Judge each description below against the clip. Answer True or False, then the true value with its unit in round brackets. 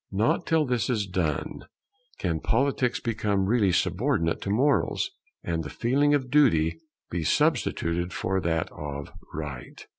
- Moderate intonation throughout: False (7.3 semitones)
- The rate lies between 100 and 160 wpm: True (140 wpm)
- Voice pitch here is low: True (100 Hz)